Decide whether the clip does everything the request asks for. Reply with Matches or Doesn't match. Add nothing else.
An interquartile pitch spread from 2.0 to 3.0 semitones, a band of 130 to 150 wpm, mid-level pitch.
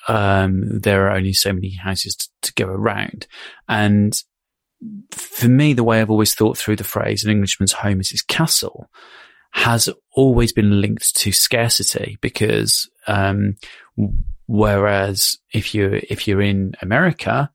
Doesn't match